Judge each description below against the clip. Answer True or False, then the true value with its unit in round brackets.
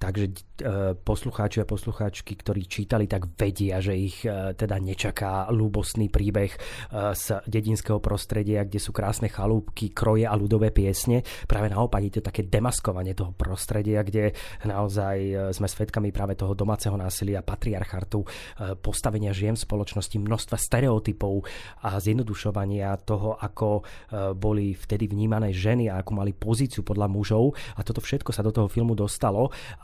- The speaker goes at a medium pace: True (140 wpm)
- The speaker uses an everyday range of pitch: False (1.7 semitones)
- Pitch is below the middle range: True (105 Hz)